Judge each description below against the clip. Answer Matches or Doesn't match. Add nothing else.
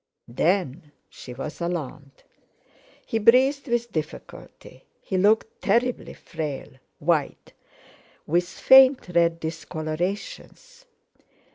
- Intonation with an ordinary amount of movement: Doesn't match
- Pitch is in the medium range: Matches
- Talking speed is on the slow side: Matches